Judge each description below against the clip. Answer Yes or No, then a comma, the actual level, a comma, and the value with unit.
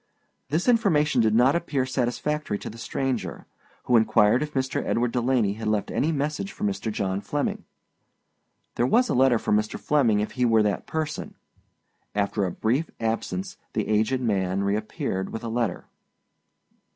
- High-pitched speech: No, low, 120 Hz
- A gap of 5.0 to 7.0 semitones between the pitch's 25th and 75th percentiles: Yes, wide, 5.5 semitones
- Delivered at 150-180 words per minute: Yes, average, 165 wpm